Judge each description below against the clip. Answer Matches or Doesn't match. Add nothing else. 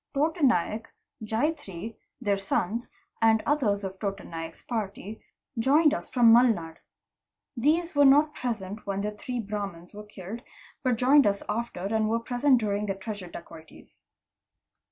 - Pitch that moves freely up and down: Doesn't match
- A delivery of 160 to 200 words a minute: Doesn't match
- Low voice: Doesn't match